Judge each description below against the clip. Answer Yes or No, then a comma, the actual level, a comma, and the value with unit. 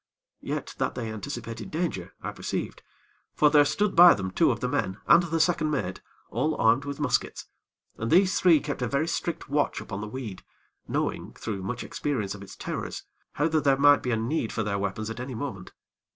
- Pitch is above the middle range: No, low, 135 Hz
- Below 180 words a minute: No, fast, 205 wpm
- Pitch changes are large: Yes, wide, 5.8 semitones